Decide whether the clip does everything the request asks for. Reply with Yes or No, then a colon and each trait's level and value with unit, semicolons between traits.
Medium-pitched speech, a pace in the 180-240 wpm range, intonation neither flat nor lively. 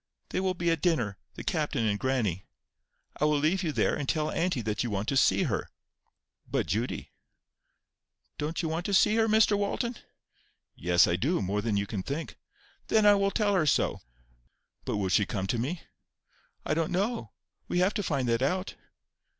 No: medium, 150 Hz; average, 190 wpm; wide, 9.0 semitones